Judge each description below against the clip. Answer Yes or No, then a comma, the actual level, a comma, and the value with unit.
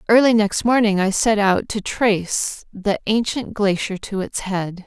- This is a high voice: Yes, high, 205 Hz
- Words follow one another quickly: No, average, 175 wpm